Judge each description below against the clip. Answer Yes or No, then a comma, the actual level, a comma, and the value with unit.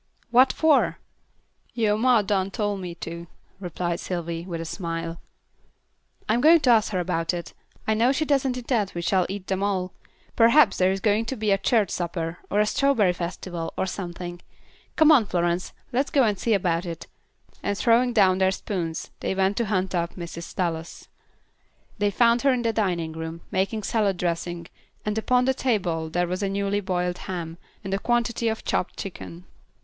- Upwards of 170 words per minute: Yes, average, 185 wpm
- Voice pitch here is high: Yes, high, 195 Hz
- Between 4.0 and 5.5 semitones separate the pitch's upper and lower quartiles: Yes, average, 4.5 semitones